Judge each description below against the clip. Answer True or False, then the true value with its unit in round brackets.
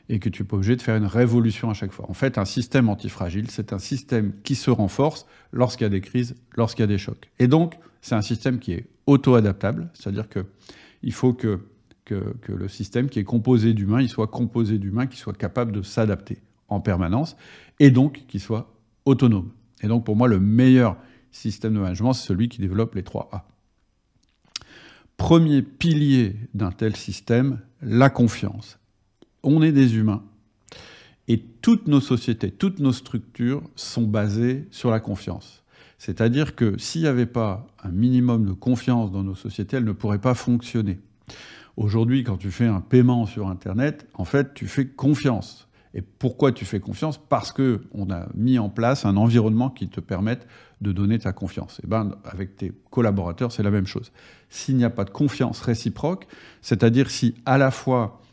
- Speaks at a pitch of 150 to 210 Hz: False (115 Hz)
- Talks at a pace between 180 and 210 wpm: True (185 wpm)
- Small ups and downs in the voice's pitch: False (3.5 semitones)